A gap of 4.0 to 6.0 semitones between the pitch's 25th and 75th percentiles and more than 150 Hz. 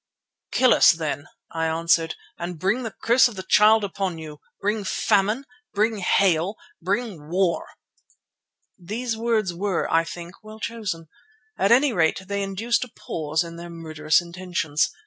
Yes: average, 4.5 semitones; high, 190 Hz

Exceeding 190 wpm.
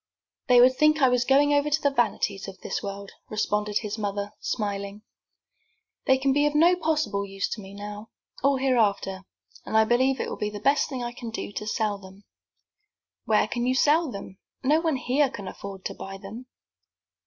Yes: average, 200 wpm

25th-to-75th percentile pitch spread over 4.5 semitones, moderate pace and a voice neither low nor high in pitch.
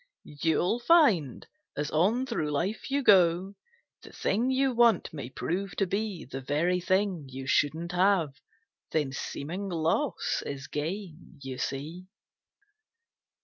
No: wide, 5.4 semitones; slow, 130 wpm; medium, 175 Hz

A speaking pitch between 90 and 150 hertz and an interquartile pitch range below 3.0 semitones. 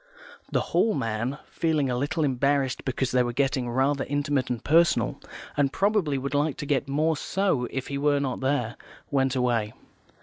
Yes: medium, 140 Hz; narrow, 2.5 semitones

